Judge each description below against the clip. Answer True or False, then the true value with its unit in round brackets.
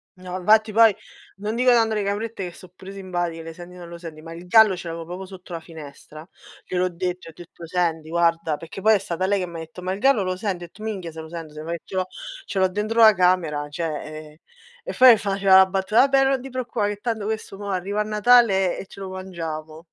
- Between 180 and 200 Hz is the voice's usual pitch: True (185 Hz)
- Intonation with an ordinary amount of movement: True (3.7 semitones)